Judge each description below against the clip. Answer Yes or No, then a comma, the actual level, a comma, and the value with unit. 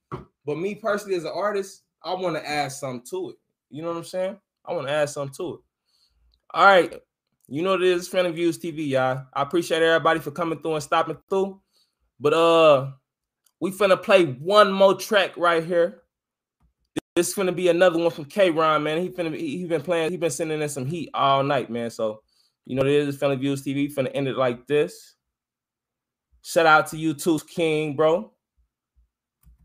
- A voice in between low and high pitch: Yes, medium, 165 Hz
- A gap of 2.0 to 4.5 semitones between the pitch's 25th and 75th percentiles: Yes, average, 3.9 semitones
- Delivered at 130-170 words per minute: No, fast, 205 wpm